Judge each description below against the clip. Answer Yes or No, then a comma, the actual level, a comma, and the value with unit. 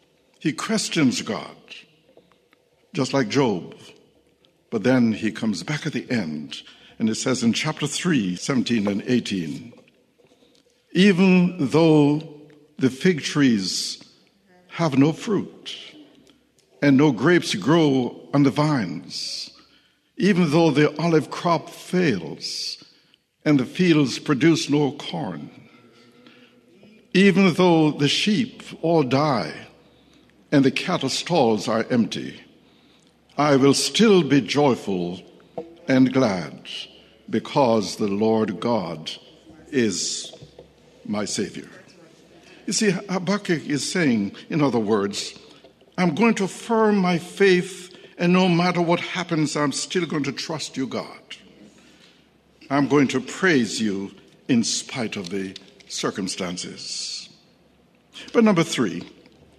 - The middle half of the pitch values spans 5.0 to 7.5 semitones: Yes, wide, 5.4 semitones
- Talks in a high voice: No, medium, 150 Hz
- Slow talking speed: Yes, slow, 115 wpm